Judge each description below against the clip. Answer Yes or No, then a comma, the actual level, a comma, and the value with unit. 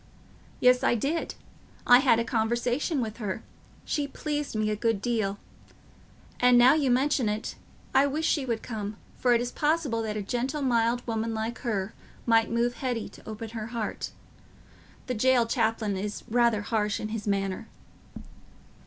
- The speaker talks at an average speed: Yes, average, 160 wpm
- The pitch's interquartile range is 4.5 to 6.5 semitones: No, narrow, 2.6 semitones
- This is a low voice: No, high, 230 Hz